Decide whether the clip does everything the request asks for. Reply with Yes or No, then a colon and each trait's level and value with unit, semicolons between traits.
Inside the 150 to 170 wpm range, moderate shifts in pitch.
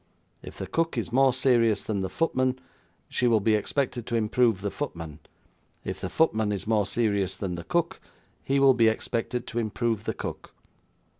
No: average, 180 wpm; average, 3.9 semitones